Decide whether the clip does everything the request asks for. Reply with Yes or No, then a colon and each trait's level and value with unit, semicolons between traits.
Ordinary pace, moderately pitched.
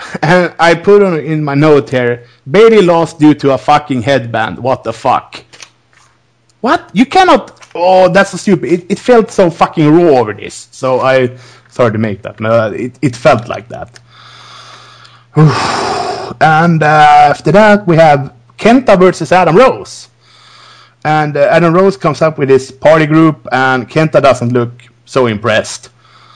Yes: average, 160 wpm; medium, 150 Hz